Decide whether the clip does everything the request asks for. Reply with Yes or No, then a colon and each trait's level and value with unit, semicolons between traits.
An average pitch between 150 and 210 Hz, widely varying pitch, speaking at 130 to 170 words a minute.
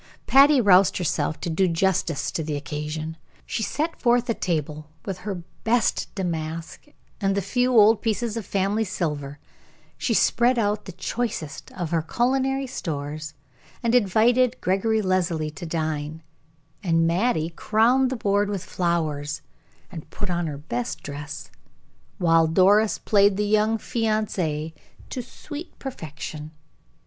Yes: medium, 185 Hz; wide, 5.8 semitones; average, 140 wpm